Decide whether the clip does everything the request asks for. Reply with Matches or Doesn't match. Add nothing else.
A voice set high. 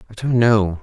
Doesn't match